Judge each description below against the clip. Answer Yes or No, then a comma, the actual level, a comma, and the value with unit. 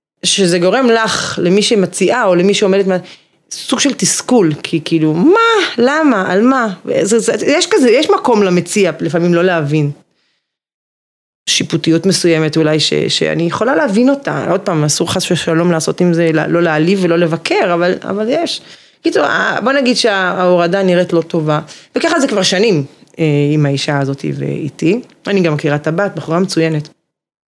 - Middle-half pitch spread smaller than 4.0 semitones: No, average, 4.7 semitones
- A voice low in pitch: No, medium, 180 Hz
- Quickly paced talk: Yes, fast, 155 wpm